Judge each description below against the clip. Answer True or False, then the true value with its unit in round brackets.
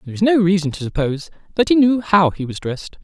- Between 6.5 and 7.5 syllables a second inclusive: True (6.9 syllables/s)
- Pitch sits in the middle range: True (180 Hz)